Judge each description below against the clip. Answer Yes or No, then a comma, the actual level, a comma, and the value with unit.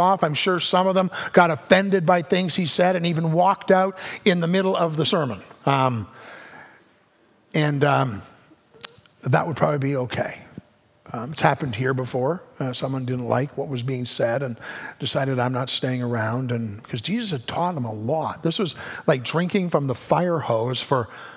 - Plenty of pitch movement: Yes, wide, 6.1 semitones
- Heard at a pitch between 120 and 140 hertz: No, medium, 150 Hz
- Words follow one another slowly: No, average, 195 wpm